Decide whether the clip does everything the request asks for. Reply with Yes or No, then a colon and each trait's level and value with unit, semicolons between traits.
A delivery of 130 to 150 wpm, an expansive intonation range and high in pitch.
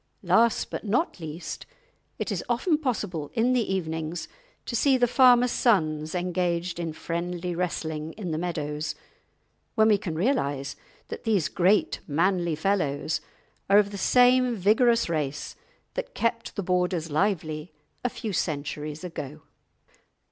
No: average, 140 wpm; wide, 6.2 semitones; medium, 180 Hz